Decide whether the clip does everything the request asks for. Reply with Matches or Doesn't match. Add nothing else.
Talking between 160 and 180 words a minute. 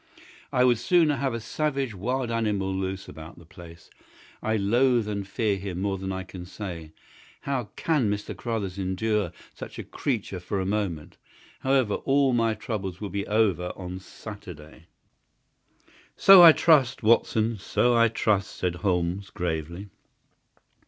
Doesn't match